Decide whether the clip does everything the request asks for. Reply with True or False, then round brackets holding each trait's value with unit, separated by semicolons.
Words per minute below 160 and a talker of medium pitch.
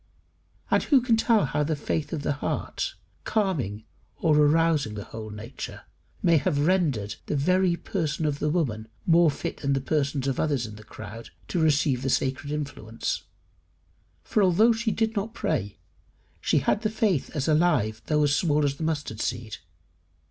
False (175 wpm; 150 Hz)